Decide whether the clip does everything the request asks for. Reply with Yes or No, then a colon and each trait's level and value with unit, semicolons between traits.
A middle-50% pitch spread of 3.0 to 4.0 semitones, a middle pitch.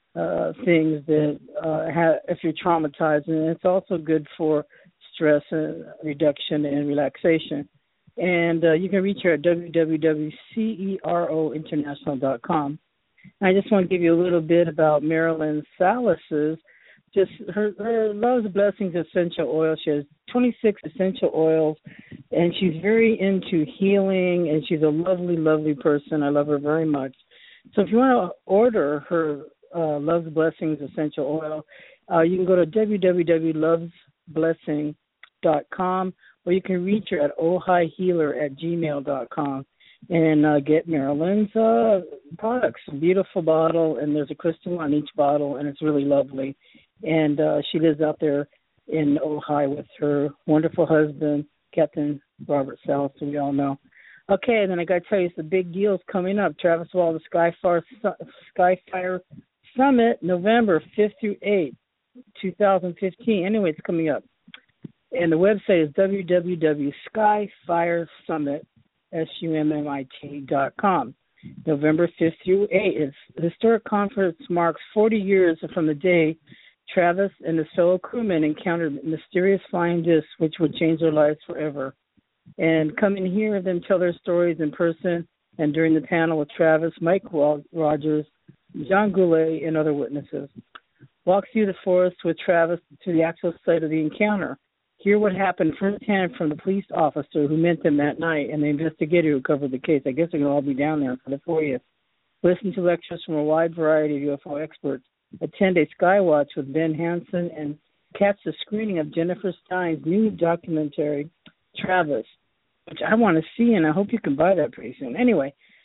Yes: average, 3.5 semitones; medium, 165 Hz